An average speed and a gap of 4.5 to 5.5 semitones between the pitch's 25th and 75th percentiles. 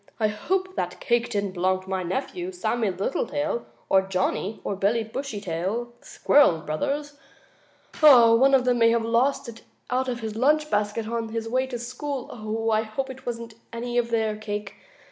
No: average, 175 wpm; average, 3.7 semitones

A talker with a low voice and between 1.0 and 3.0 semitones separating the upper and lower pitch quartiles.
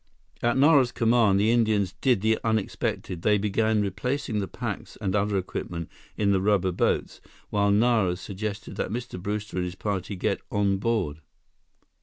Yes: low, 105 Hz; narrow, 2.6 semitones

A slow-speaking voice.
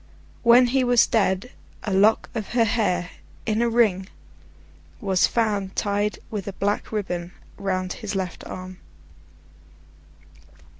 Yes: slow, 130 wpm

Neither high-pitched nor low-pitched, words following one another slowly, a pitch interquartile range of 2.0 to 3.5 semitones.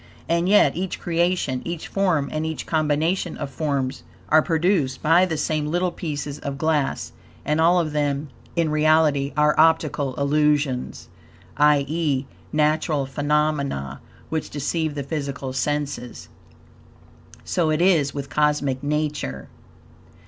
Yes: medium, 150 Hz; slow, 125 wpm; narrow, 2.4 semitones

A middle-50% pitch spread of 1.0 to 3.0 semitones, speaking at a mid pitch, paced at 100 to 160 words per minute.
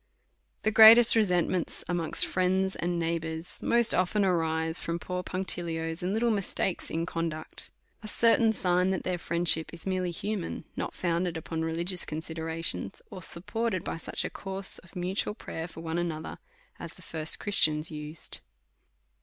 Yes: average, 2.7 semitones; medium, 175 Hz; average, 155 wpm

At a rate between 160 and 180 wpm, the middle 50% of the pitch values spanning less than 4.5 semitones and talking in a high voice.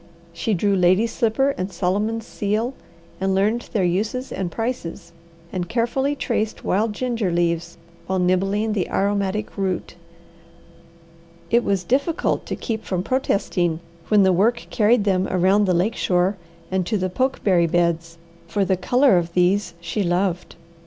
No: average, 150 wpm; average, 3.7 semitones; high, 195 Hz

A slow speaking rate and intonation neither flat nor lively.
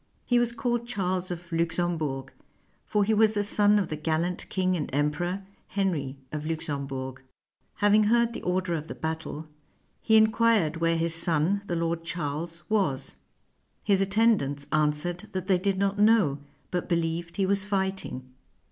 No: average, 160 wpm; average, 4.2 semitones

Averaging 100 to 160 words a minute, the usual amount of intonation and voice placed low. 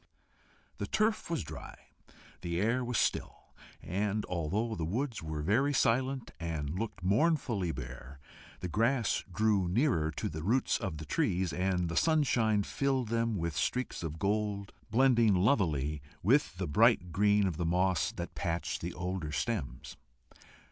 No: average, 150 wpm; wide, 5.8 semitones; low, 100 Hz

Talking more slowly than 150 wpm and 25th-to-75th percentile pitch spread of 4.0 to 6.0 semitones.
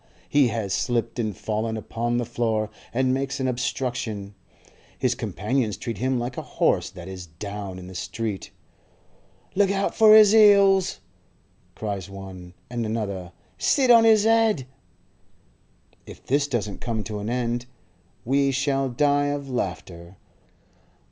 Yes: average, 140 wpm; average, 5.2 semitones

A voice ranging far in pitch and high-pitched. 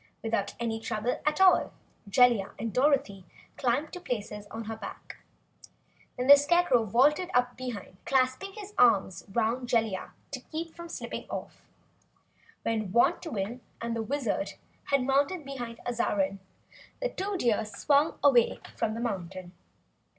No: average, 4.7 semitones; high, 245 Hz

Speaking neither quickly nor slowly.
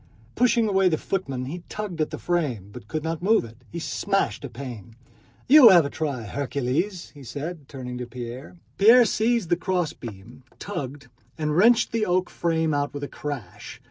Yes: average, 180 wpm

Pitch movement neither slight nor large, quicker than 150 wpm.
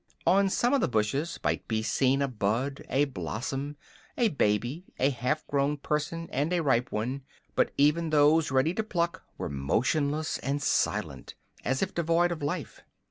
Yes: average, 4.4 semitones; average, 170 wpm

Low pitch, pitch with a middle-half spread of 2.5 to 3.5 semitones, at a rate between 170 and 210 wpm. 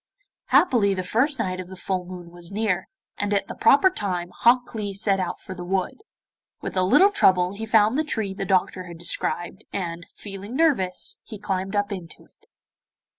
No: high, 195 Hz; average, 3.2 semitones; average, 190 wpm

